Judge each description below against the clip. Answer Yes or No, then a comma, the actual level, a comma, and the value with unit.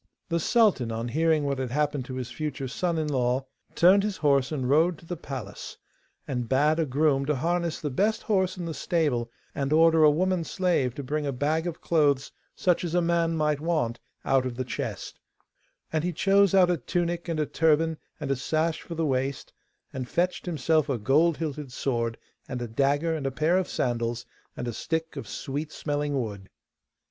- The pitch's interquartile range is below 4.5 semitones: Yes, average, 4.1 semitones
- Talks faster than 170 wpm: Yes, average, 200 wpm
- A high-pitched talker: No, medium, 150 Hz